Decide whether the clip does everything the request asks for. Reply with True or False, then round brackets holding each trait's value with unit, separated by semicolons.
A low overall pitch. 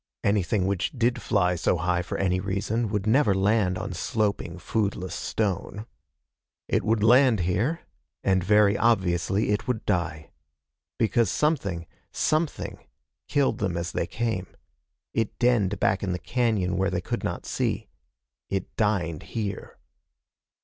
True (100 Hz)